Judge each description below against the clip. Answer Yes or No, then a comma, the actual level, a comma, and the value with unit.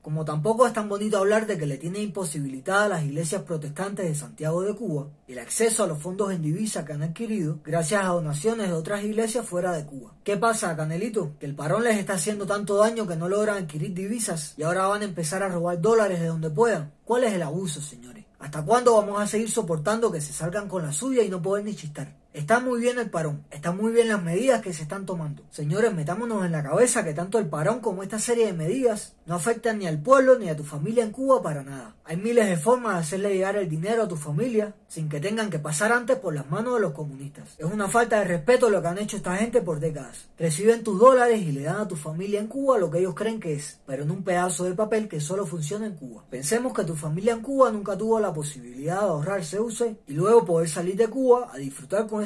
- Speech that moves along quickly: Yes, fast, 245 wpm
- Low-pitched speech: No, high, 195 Hz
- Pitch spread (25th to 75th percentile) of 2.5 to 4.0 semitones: No, average, 5.2 semitones